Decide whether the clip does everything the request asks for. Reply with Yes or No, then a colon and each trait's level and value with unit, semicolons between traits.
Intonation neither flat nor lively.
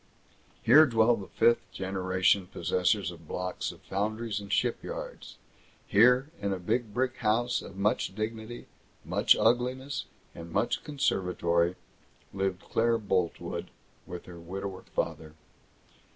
Yes: average, 4.3 semitones